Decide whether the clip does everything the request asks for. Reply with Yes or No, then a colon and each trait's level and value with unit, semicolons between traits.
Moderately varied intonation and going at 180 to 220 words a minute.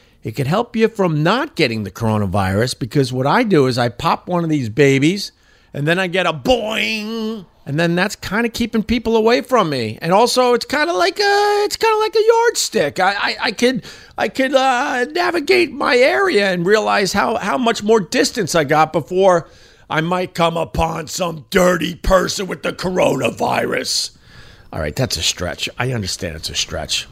No: wide, 8.1 semitones; average, 195 wpm